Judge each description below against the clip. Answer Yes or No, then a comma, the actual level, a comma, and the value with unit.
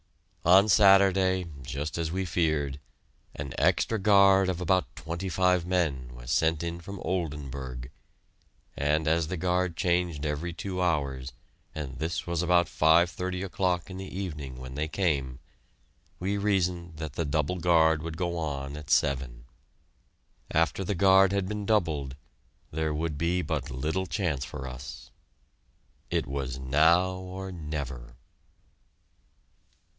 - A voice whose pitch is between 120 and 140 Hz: No, very low, 85 Hz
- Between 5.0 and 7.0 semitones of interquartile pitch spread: No, average, 4.2 semitones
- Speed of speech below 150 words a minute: Yes, average, 140 wpm